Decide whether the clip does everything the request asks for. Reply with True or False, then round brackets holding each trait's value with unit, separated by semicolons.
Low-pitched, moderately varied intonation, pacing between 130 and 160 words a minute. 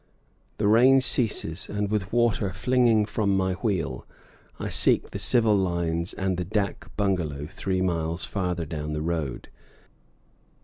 True (95 Hz; 4.1 semitones; 140 wpm)